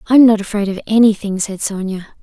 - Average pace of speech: Yes, average, 190 wpm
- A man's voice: No, female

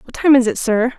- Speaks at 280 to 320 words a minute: Yes, fast, 305 wpm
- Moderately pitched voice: No, very high, 250 Hz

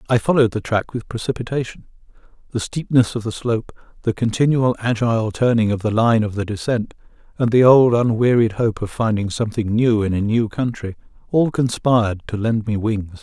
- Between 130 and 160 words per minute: No, average, 180 wpm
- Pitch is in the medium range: No, low, 115 Hz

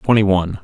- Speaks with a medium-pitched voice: No, low, 100 Hz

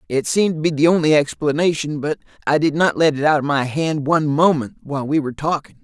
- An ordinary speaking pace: No, fast, 235 wpm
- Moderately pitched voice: Yes, medium, 150 Hz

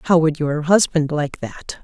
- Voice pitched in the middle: Yes, medium, 155 Hz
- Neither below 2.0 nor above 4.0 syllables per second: Yes, 3.9 syllables/s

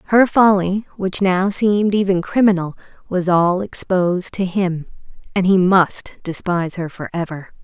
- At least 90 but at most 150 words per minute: Yes, average, 140 wpm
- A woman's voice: Yes, female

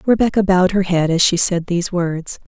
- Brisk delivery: Yes, fast, 210 wpm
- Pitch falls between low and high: Yes, medium, 180 Hz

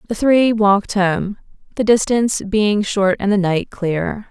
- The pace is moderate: Yes, average, 165 wpm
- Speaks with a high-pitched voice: Yes, high, 205 Hz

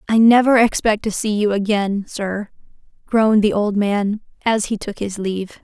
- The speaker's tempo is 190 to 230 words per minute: No, average, 180 wpm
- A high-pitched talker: Yes, high, 210 Hz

